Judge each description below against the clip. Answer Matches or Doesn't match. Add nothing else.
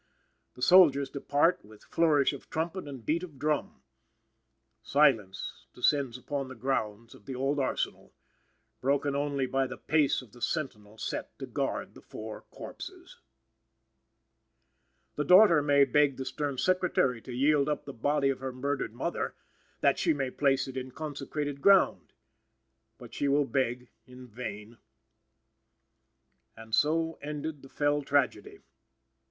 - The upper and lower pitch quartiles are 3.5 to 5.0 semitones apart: Doesn't match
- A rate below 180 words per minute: Matches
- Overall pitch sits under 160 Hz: Matches